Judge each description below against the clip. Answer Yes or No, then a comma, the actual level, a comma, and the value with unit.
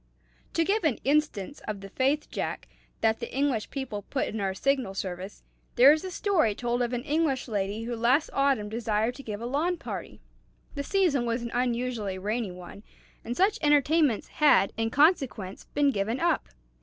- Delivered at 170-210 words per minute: Yes, average, 180 wpm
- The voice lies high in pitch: Yes, high, 245 Hz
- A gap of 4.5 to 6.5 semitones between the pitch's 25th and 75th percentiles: Yes, wide, 5.4 semitones